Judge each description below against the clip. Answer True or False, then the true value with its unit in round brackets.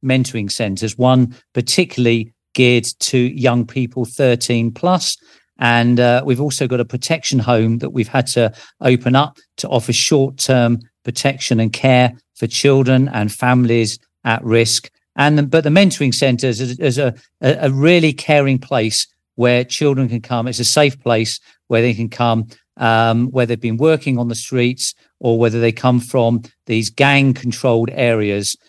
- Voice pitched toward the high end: False (125 Hz)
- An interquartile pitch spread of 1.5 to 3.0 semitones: True (2.4 semitones)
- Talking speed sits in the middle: True (165 wpm)